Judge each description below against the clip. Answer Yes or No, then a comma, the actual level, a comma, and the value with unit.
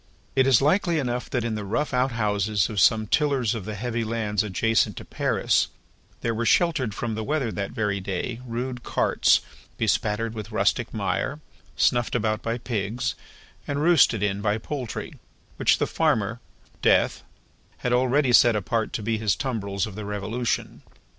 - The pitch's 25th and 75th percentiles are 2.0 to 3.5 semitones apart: Yes, average, 3.0 semitones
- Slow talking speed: No, average, 165 wpm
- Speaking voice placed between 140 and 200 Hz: No, low, 115 Hz